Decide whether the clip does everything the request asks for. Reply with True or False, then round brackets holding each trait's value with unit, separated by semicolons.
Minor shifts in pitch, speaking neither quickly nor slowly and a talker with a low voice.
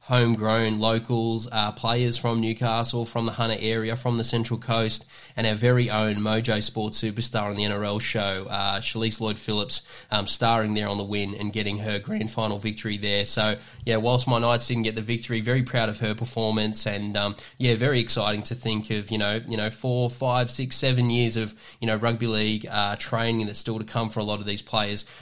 False (1.6 semitones; 215 wpm; 110 Hz)